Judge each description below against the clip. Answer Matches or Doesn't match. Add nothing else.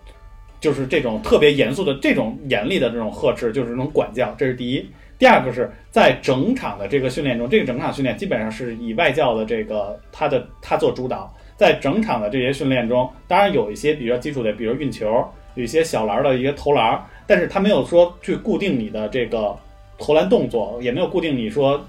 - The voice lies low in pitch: Matches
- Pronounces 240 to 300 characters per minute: Doesn't match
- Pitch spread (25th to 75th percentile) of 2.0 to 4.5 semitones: Doesn't match